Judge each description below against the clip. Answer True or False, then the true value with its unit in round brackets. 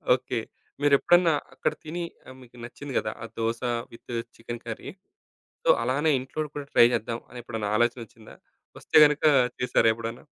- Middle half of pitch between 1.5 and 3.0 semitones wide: False (3.8 semitones)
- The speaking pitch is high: False (120 Hz)